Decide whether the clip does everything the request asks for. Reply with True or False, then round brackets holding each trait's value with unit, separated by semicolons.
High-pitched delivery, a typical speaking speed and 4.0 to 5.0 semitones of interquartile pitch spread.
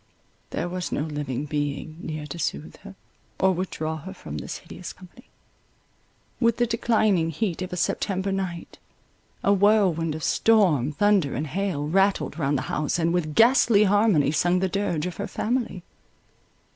False (180 Hz; 160 wpm; 4.7 semitones)